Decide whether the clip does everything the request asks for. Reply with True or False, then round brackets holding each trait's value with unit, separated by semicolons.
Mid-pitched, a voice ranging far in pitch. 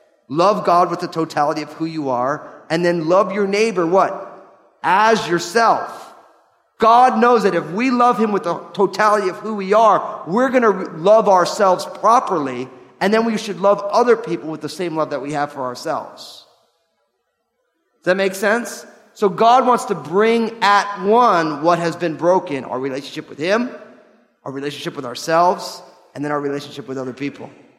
True (180 Hz; 5.7 semitones)